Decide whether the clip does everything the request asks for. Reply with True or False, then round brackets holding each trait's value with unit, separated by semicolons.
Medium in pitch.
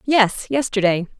False (220 Hz)